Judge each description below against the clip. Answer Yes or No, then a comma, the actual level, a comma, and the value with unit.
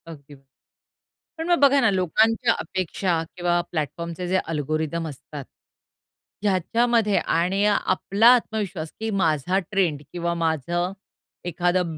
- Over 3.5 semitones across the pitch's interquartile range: Yes, average, 4.0 semitones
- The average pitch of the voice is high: No, medium, 180 Hz